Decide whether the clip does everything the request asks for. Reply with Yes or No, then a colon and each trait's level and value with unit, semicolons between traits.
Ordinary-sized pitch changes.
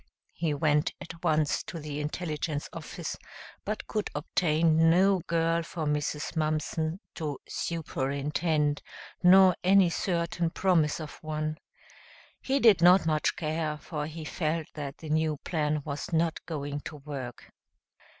No: narrow, 2.1 semitones